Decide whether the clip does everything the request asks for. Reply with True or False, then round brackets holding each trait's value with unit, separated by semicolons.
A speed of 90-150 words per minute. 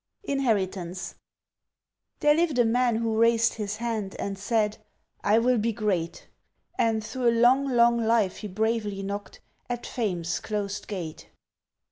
True (140 wpm)